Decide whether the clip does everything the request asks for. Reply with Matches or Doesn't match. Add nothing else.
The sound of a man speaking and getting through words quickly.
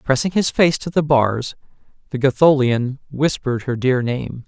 Doesn't match